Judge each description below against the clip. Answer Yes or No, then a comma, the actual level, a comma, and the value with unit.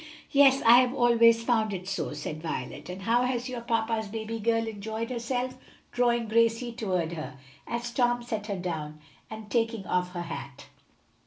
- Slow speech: No, average, 170 wpm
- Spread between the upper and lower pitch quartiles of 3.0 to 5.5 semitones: Yes, average, 4.2 semitones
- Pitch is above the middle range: Yes, high, 225 Hz